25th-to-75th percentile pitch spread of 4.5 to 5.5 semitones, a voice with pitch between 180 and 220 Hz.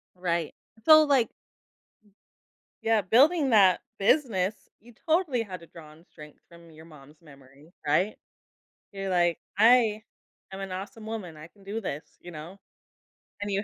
Yes: average, 5.1 semitones; high, 190 Hz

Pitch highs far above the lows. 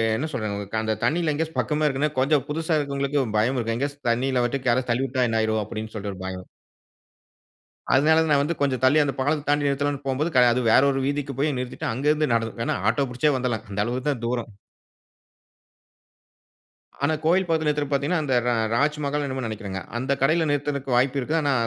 No: average, 3.6 semitones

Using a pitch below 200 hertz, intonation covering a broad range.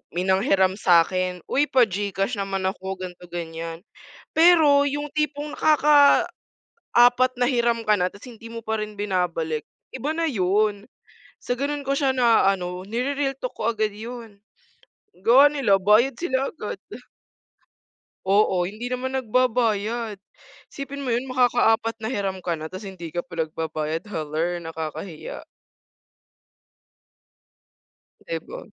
No: high, 215 Hz; wide, 5.9 semitones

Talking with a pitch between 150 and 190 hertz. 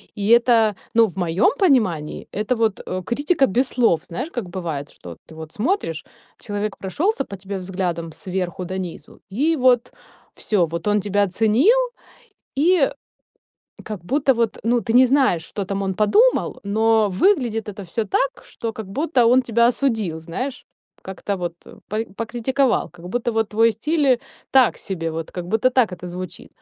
No: high, 215 Hz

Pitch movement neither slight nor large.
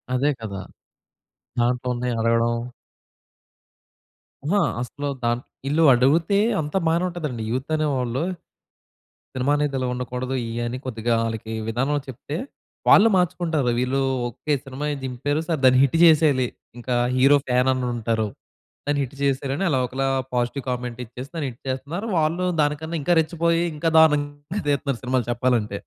Yes: average, 3.3 semitones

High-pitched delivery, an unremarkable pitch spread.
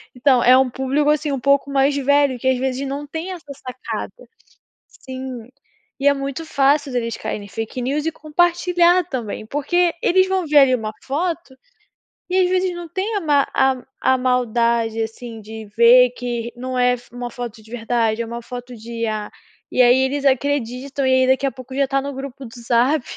Yes: very high, 260 Hz; average, 3.0 semitones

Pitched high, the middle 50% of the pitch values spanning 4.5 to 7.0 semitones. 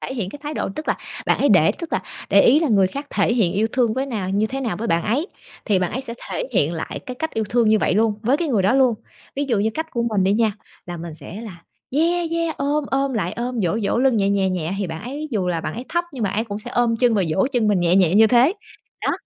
Yes: high, 225 Hz; average, 5.2 semitones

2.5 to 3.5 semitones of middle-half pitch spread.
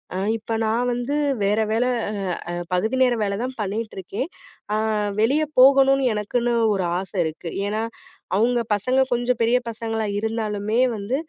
Yes: average, 3.1 semitones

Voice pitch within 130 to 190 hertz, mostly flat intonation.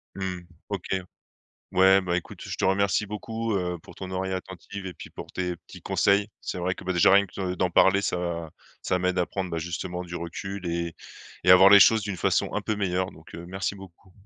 No: very low, 95 Hz; narrow, 1.8 semitones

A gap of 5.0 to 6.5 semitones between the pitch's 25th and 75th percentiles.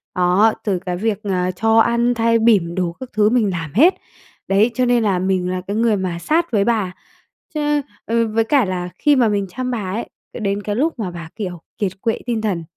No: average, 4.1 semitones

